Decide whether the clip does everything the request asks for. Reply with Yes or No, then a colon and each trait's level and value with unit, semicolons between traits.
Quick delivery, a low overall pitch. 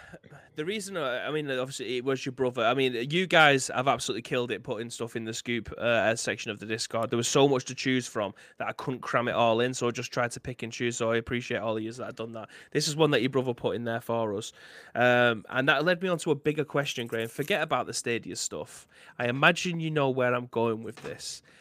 Yes: fast, 265 wpm; low, 125 Hz